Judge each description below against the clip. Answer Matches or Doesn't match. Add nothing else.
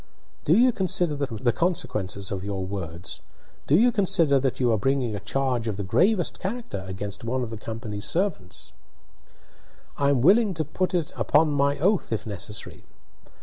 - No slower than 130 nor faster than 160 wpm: Doesn't match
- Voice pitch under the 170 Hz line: Matches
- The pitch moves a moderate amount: Doesn't match